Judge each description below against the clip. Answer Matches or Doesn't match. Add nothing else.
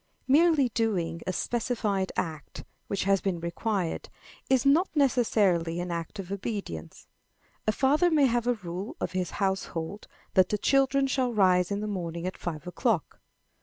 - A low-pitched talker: Doesn't match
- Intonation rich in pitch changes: Matches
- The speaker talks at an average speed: Matches